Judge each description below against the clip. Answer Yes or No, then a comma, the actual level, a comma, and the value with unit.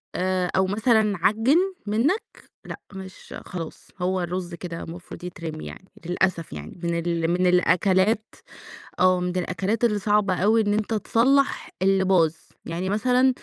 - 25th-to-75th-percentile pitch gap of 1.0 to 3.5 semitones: Yes, average, 3.2 semitones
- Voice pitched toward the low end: No, medium, 185 Hz